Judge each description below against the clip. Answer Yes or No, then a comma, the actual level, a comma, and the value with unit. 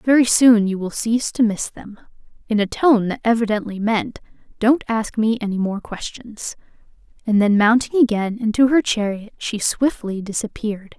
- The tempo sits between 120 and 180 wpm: Yes, average, 165 wpm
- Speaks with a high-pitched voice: Yes, high, 220 Hz